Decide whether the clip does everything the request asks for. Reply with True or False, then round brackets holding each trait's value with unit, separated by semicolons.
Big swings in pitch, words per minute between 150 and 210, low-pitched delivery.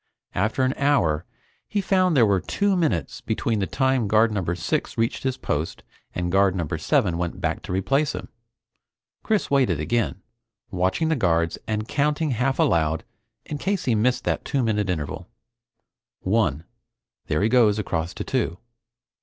True (7.3 semitones; 160 wpm; 110 Hz)